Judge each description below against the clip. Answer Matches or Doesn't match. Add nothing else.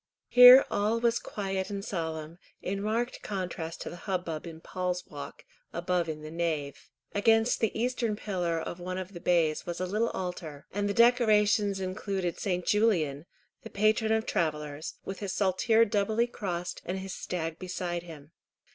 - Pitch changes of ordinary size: Matches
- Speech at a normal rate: Matches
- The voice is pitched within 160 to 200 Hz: Matches